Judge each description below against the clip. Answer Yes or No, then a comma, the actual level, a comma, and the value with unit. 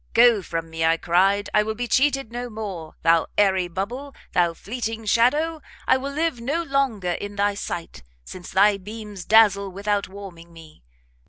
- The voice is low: No, high, 205 Hz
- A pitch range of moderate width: Yes, average, 4.9 semitones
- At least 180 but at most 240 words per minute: No, average, 170 wpm